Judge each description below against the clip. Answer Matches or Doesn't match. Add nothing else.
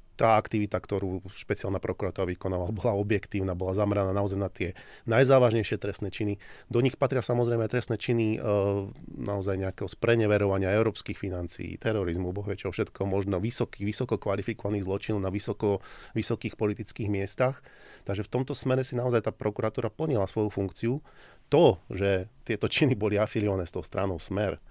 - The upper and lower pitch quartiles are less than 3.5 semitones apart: Matches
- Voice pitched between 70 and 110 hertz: Matches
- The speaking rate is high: Doesn't match